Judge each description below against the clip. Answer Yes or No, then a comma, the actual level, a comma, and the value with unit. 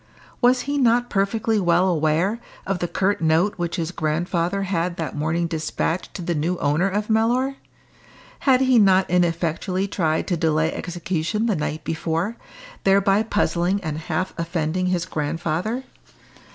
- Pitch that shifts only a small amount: No, average, 3.7 semitones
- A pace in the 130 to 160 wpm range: Yes, average, 150 wpm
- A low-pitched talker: No, medium, 180 Hz